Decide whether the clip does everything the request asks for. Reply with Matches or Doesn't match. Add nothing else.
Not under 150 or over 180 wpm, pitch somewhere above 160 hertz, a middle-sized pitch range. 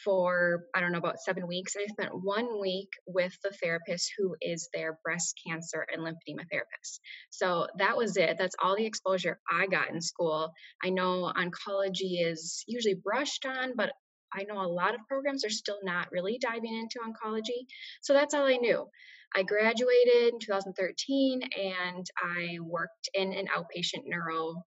Matches